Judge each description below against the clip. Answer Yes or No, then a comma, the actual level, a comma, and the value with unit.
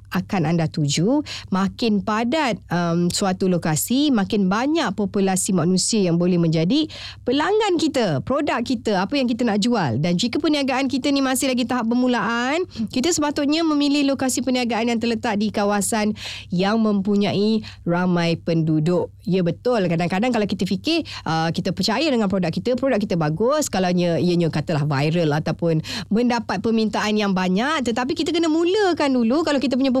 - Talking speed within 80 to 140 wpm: No, fast, 155 wpm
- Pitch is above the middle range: Yes, high, 215 Hz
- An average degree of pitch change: No, wide, 6.5 semitones